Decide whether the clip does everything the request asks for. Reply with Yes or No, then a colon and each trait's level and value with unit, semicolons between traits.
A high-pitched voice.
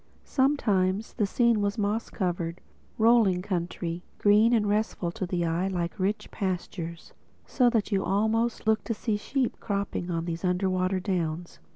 Yes: high, 195 Hz